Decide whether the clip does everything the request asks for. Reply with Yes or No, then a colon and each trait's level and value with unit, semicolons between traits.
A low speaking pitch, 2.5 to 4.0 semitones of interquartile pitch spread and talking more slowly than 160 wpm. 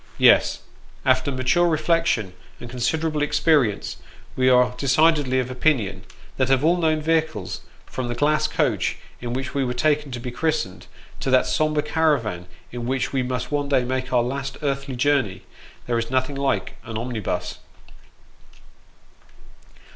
Yes: low, 130 Hz; average, 3.5 semitones; average, 150 wpm